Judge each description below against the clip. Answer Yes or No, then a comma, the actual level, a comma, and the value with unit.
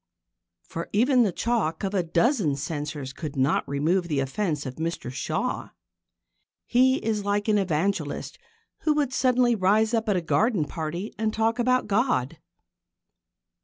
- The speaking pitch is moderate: No, high, 195 Hz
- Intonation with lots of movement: Yes, wide, 6.5 semitones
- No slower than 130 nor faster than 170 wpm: Yes, average, 150 wpm